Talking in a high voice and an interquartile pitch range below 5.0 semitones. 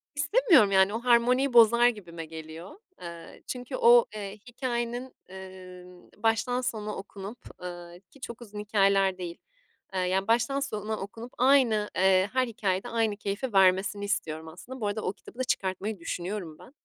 Yes: high, 210 Hz; average, 4.2 semitones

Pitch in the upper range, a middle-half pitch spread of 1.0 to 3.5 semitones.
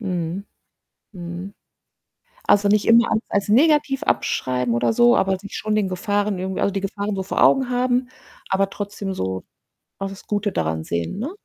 Yes: high, 200 Hz; average, 2.8 semitones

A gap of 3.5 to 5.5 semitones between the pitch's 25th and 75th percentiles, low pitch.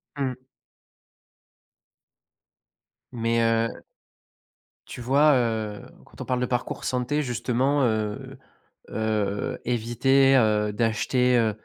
No: average, 2.9 semitones; low, 120 Hz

